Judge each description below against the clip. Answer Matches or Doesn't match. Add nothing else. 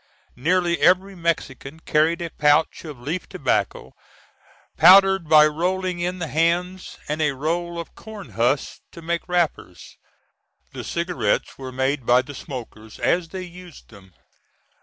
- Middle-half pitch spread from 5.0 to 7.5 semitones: Doesn't match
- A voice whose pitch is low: Doesn't match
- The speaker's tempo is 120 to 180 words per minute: Matches